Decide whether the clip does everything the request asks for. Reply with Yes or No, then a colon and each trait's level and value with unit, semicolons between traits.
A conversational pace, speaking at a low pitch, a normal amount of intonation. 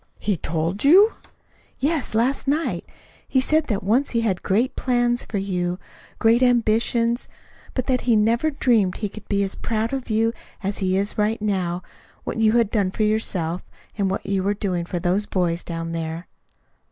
No: average, 180 wpm; high, 215 Hz; average, 4.3 semitones